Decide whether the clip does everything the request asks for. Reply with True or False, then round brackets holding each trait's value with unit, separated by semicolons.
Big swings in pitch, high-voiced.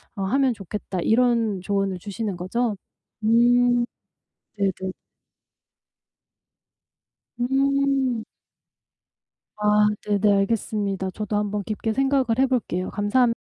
False (3.6 semitones; 215 Hz)